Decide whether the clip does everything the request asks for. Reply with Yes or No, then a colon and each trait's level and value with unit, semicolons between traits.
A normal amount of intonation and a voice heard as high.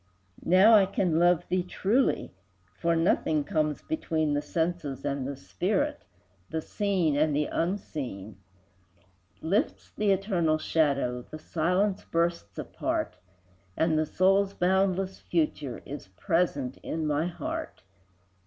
No: average, 4.1 semitones; medium, 165 Hz